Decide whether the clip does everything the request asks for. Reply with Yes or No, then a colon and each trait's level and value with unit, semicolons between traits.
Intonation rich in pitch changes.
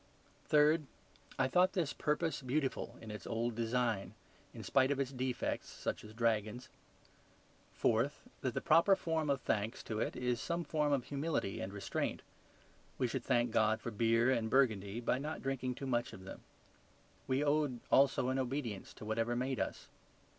No: average, 3.8 semitones